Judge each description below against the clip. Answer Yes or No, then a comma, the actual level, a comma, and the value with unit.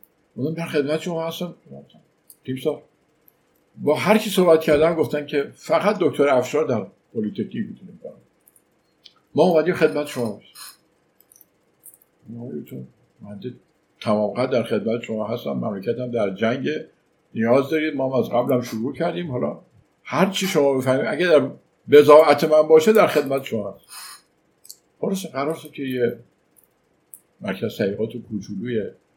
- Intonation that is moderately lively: Yes, average, 4.7 semitones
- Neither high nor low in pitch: Yes, medium, 145 Hz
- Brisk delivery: No, average, 115 wpm